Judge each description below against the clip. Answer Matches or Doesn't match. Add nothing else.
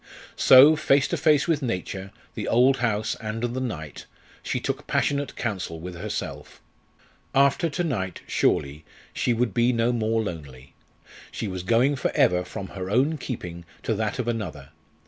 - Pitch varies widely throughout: Matches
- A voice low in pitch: Matches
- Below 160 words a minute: Doesn't match